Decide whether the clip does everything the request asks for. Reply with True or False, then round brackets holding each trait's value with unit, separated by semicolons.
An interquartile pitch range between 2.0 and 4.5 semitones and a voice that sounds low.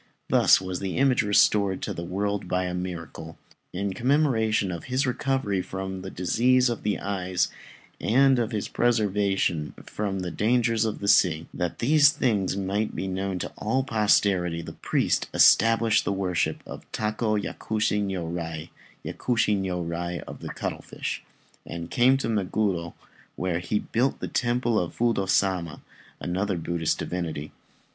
True (4.1 semitones; 100 Hz)